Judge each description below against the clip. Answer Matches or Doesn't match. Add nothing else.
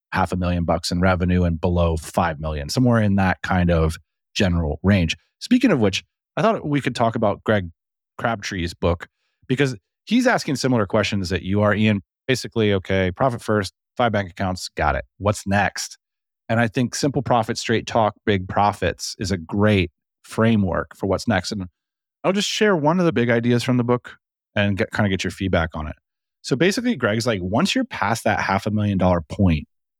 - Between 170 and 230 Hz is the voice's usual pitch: Doesn't match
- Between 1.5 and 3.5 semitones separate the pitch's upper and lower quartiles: Doesn't match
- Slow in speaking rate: Doesn't match